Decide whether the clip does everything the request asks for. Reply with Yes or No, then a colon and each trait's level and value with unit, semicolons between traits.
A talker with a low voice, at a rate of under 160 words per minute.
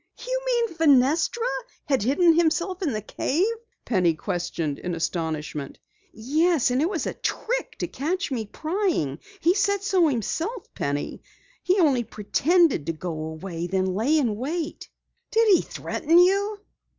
No: very high, 295 Hz; average, 145 wpm